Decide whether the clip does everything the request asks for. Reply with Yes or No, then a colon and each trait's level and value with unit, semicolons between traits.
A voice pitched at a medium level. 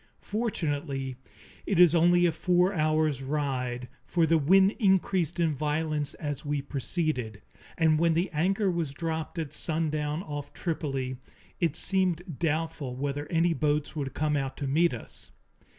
Yes: medium, 155 Hz